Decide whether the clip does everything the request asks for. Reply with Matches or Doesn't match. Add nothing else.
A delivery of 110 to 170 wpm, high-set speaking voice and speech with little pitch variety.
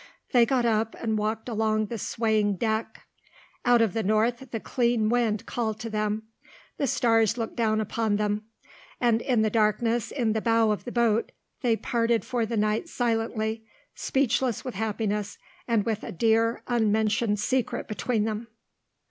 Matches